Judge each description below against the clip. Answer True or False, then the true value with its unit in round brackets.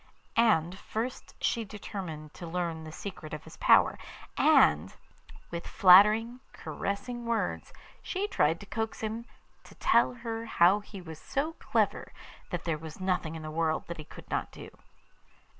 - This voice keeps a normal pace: True (160 wpm)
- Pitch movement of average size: False (5.7 semitones)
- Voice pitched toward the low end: False (190 Hz)